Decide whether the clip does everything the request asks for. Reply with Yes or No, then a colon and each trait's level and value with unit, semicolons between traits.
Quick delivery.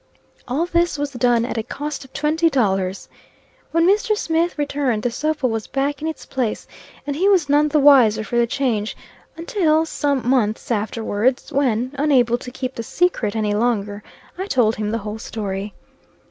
No: average, 175 wpm